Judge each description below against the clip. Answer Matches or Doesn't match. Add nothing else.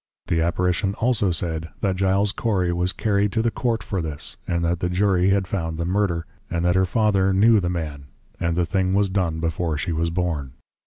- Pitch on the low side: Matches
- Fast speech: Matches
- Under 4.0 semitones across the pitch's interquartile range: Matches